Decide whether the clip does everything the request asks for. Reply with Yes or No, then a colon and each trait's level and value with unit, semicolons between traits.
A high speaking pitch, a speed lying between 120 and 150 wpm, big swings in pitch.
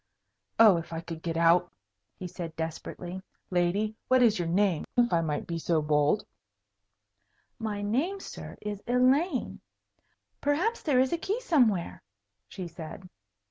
Yes: high, 195 Hz; average, 145 wpm; wide, 6.9 semitones